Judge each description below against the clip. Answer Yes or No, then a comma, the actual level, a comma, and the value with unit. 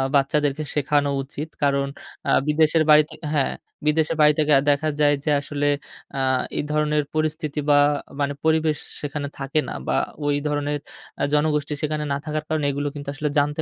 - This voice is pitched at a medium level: Yes, medium, 150 Hz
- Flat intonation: Yes, narrow, 1.1 semitones